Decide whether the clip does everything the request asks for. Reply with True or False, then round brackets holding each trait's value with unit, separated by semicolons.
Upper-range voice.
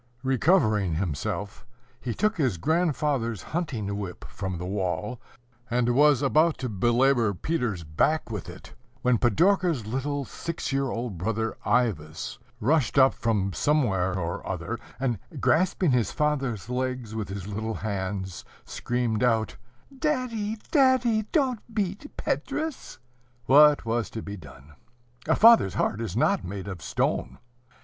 False (120 Hz)